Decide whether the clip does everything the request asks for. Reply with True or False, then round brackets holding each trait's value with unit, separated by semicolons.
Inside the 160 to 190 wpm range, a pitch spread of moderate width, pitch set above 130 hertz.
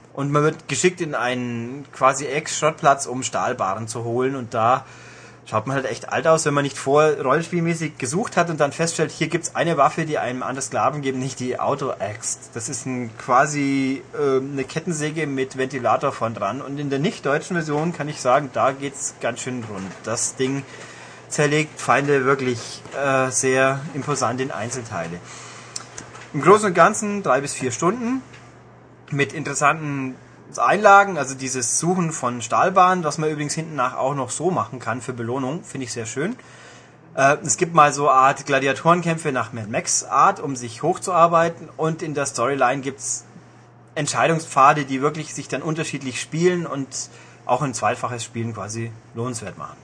True (175 wpm; 3.5 semitones; 140 Hz)